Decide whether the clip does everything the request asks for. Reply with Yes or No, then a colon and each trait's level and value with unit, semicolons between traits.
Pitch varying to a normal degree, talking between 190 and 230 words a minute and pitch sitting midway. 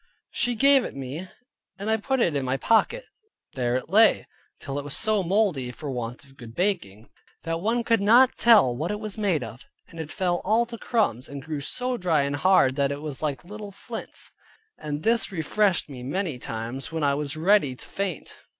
No: wide, 7.5 semitones; fast, 205 wpm; medium, 165 Hz